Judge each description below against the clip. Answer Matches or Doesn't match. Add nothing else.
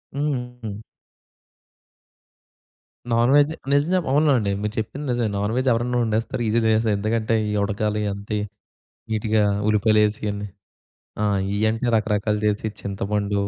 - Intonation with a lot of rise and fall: Doesn't match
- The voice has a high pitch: Doesn't match